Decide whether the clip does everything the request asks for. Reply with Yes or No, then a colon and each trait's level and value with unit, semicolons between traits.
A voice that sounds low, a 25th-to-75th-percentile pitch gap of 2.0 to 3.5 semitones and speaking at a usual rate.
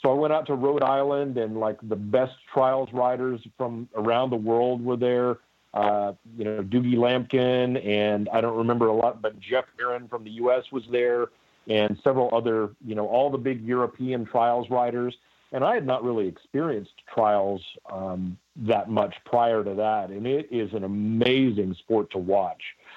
Yes: low, 120 Hz; average, 2.8 semitones; average, 185 wpm